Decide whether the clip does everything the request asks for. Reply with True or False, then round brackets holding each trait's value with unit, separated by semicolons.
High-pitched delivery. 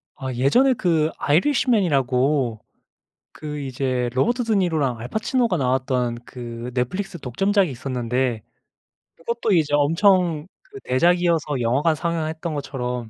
False (145 Hz)